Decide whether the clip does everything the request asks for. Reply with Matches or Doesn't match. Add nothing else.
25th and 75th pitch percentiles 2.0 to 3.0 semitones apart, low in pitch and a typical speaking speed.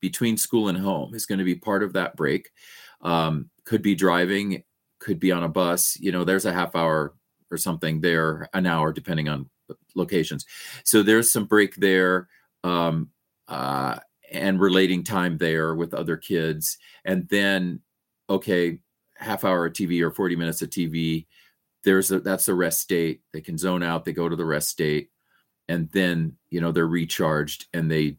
Matches